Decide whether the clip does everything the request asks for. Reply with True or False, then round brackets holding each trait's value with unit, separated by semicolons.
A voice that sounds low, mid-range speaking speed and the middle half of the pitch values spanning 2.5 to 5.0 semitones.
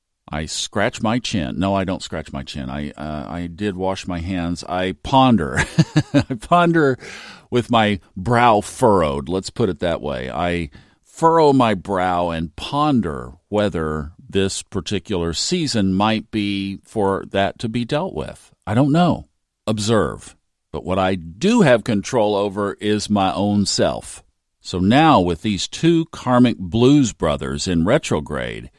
False (100 Hz; 150 wpm; 5.4 semitones)